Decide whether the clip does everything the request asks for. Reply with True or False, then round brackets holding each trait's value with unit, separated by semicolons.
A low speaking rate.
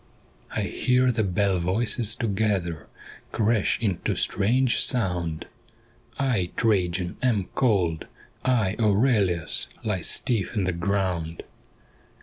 True (120 wpm)